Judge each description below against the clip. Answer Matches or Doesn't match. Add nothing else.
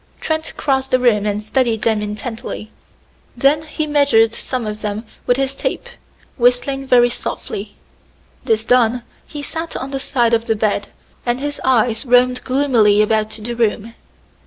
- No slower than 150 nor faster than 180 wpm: Matches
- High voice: Matches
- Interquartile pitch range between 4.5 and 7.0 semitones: Doesn't match